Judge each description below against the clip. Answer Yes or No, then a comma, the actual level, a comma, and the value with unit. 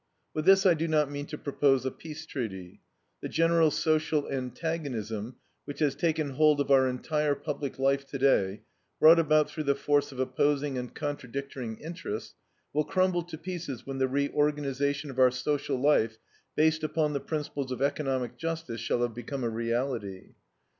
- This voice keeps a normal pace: Yes, average, 165 wpm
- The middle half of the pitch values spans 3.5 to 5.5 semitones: No, average, 3.1 semitones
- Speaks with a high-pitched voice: No, medium, 140 Hz